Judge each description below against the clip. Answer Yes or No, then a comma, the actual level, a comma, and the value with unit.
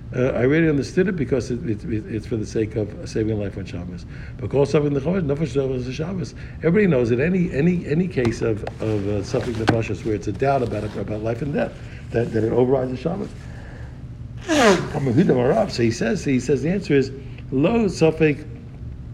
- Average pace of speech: Yes, average, 190 wpm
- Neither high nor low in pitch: No, low, 125 Hz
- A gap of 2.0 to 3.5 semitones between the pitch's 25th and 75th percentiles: No, average, 5.1 semitones